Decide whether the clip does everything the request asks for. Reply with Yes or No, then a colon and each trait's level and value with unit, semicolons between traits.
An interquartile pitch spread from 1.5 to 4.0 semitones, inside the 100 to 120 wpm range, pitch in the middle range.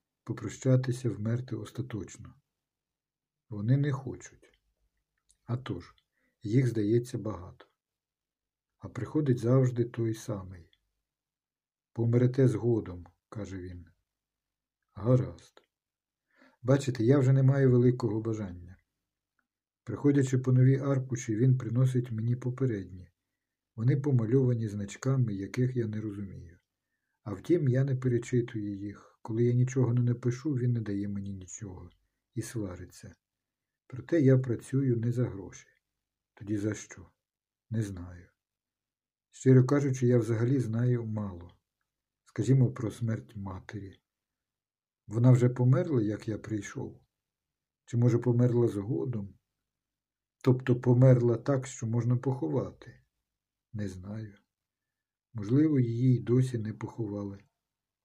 No: average, 3.7 semitones; average, 110 wpm; low, 120 Hz